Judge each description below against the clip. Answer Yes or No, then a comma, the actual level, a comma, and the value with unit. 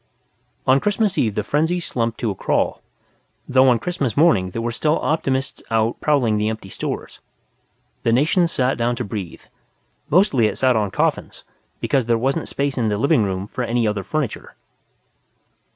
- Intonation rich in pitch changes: No, average, 4.7 semitones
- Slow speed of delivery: No, average, 170 wpm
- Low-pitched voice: Yes, low, 120 Hz